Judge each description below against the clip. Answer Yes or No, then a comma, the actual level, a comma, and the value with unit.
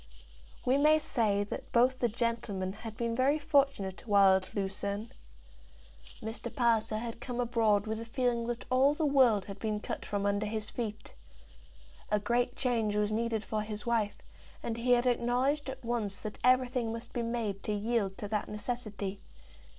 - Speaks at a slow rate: No, average, 175 wpm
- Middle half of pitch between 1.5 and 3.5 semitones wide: Yes, average, 2.9 semitones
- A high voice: Yes, high, 230 Hz